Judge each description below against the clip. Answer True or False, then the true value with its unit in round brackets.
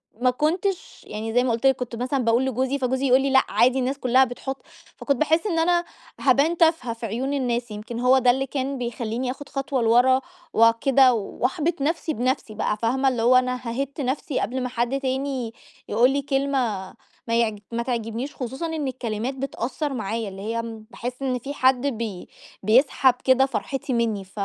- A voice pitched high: True (255 Hz)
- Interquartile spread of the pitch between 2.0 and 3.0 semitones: True (2.7 semitones)